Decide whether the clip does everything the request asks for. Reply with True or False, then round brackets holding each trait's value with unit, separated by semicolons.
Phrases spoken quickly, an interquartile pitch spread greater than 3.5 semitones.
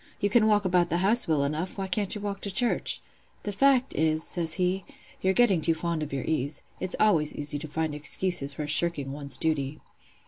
True (210 wpm; 4.7 semitones)